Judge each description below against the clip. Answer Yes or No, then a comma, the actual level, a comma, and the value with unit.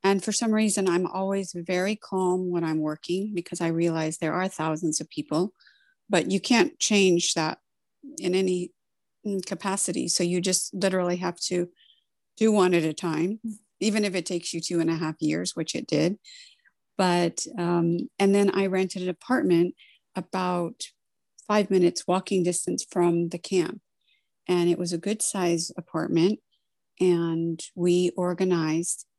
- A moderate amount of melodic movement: No, narrow, 2.3 semitones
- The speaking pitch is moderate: Yes, medium, 180 Hz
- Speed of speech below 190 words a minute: Yes, average, 160 wpm